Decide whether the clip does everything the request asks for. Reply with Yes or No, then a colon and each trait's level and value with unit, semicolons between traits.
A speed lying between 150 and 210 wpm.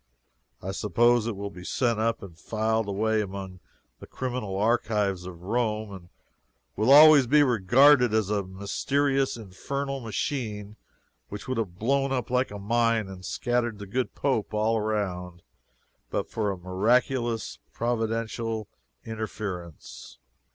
No: slow, 135 wpm